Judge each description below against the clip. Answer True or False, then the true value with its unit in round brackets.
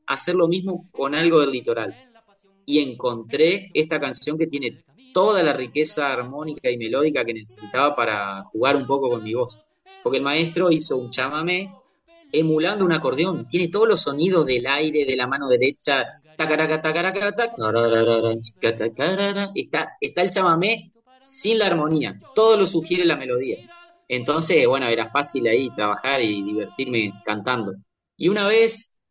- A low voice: False (155 Hz)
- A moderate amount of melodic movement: False (7.3 semitones)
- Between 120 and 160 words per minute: True (145 wpm)